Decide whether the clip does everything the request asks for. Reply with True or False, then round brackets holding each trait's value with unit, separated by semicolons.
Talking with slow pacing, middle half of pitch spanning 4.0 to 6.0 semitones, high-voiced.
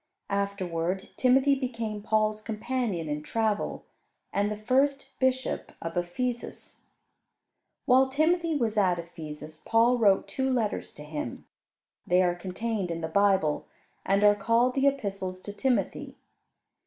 True (130 wpm; 5.6 semitones; 210 Hz)